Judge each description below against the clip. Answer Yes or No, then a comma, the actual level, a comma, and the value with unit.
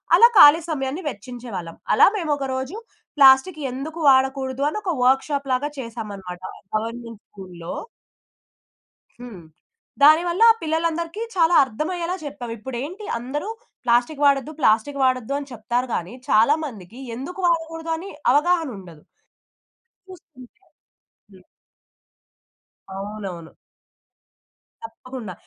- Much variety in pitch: Yes, wide, 5.7 semitones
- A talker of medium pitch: No, very high, 265 Hz